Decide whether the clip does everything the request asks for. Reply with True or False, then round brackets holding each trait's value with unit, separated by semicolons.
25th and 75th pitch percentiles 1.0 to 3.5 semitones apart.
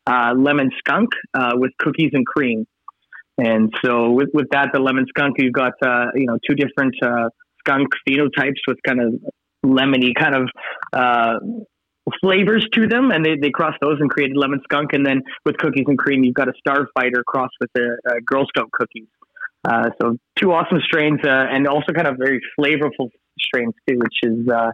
True (3.0 semitones)